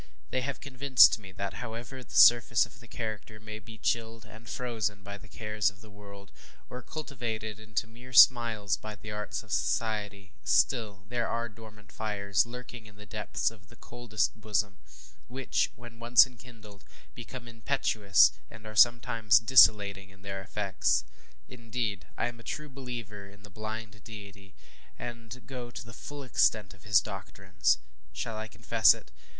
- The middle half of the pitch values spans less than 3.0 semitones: Yes, narrow, 2.6 semitones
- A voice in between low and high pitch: No, low, 110 Hz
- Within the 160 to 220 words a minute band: Yes, average, 165 wpm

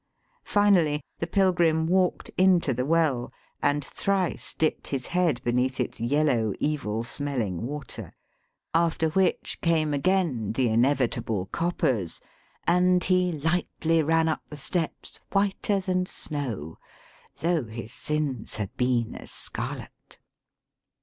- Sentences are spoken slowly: Yes, slow, 125 wpm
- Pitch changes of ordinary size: No, wide, 5.8 semitones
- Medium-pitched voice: Yes, medium, 150 Hz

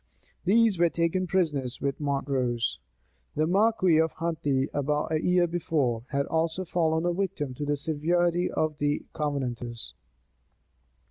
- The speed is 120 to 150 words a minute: Yes, slow, 135 wpm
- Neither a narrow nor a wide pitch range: Yes, average, 3.7 semitones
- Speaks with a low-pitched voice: No, medium, 155 Hz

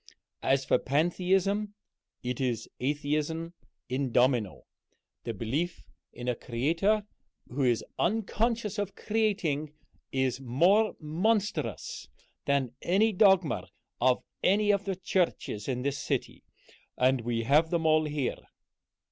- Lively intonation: Yes, wide, 7.2 semitones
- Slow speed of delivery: Yes, slow, 120 wpm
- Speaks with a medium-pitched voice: Yes, medium, 155 Hz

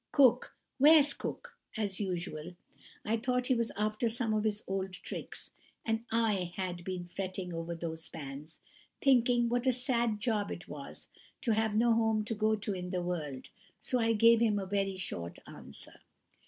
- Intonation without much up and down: No, average, 4.3 semitones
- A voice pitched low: No, high, 210 Hz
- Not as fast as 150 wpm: No, average, 175 wpm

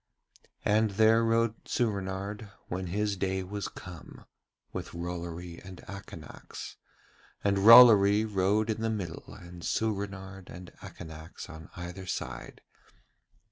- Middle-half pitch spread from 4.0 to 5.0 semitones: No, average, 3.2 semitones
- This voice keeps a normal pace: No, slow, 115 wpm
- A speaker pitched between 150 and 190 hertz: No, very low, 95 Hz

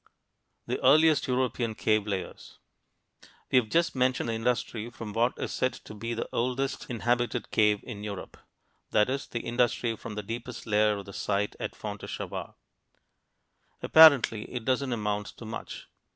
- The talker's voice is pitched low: Yes, low, 115 Hz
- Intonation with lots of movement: No, average, 3.0 semitones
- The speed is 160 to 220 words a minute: No, average, 150 wpm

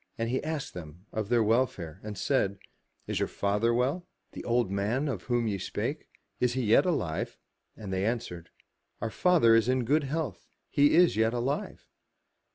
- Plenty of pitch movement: No, average, 4.7 semitones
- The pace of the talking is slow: No, average, 190 wpm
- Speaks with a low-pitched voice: Yes, low, 115 Hz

